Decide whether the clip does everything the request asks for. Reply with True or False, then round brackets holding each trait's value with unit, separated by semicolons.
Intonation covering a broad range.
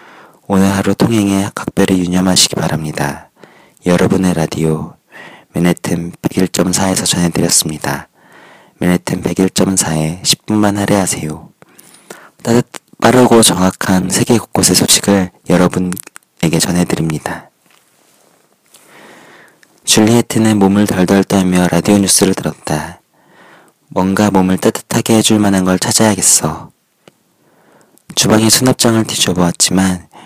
False (2.7 semitones)